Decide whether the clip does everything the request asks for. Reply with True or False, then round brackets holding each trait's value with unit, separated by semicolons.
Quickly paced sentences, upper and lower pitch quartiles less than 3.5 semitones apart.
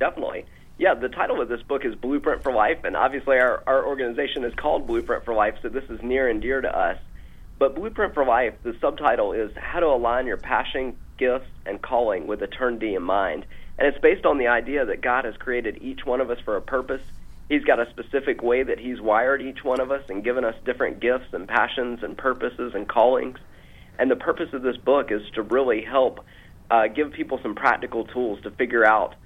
False (225 wpm; 4.6 semitones)